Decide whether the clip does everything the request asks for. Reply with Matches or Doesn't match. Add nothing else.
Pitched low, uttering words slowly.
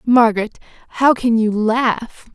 Doesn't match